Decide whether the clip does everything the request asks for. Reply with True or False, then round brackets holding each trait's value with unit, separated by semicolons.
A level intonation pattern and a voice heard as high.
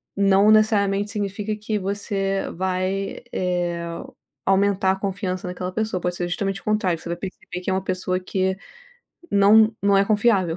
True (1.7 semitones; 195 Hz)